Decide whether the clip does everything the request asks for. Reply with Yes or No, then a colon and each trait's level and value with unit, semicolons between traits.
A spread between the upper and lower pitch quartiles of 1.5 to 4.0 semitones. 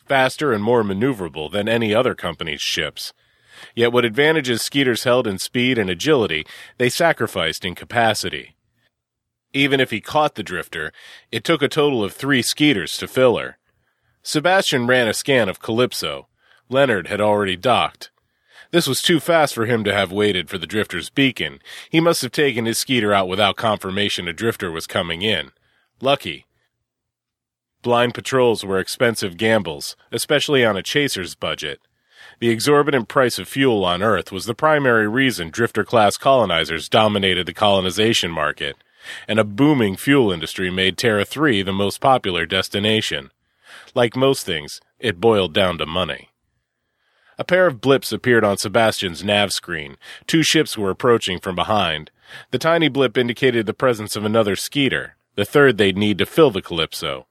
No: average, 5.1 semitones